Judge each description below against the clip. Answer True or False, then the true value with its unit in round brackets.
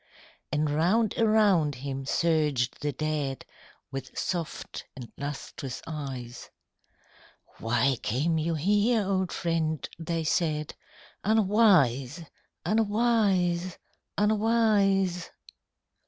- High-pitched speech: False (165 Hz)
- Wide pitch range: True (6.1 semitones)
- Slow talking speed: True (85 wpm)